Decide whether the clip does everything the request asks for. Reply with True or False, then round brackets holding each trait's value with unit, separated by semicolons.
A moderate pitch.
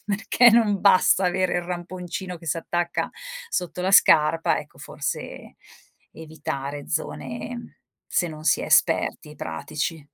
True (175 Hz)